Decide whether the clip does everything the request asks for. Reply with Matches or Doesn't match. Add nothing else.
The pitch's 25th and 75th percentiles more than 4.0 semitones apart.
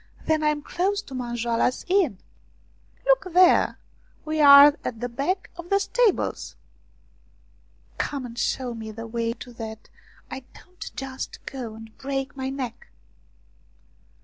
Matches